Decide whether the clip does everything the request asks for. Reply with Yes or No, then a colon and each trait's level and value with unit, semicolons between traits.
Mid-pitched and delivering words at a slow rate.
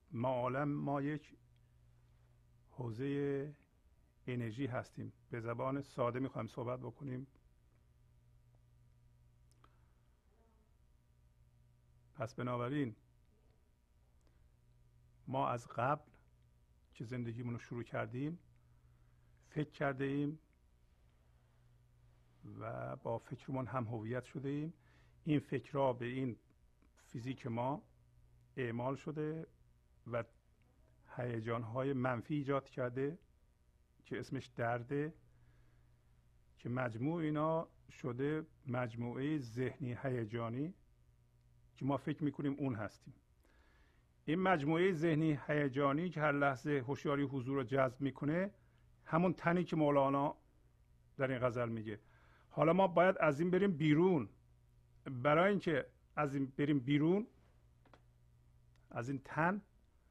No: low, 120 Hz; slow, 100 wpm